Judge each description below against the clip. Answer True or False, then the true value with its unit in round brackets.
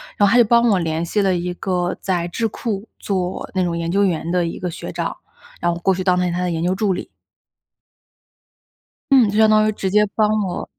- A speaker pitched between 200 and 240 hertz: False (185 Hz)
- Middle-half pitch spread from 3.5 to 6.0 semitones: False (3.1 semitones)